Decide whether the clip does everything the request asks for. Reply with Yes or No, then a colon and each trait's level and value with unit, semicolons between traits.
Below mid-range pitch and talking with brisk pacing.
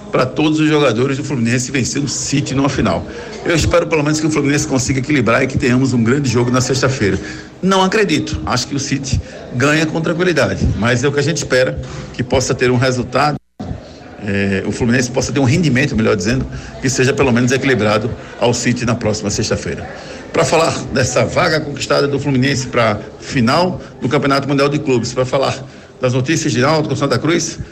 Yes: low, 130 Hz; fast, 195 wpm